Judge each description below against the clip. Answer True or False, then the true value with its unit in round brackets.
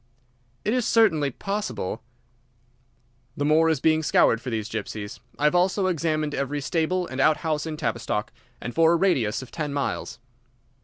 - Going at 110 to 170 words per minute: True (165 wpm)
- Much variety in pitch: False (4.2 semitones)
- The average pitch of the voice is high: False (155 Hz)